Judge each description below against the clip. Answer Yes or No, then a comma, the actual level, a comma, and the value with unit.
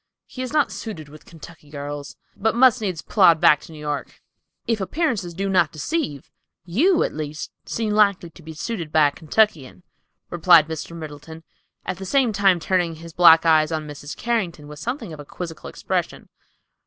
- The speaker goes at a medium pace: Yes, average, 180 wpm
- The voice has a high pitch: No, medium, 170 Hz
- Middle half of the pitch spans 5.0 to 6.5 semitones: Yes, average, 5.3 semitones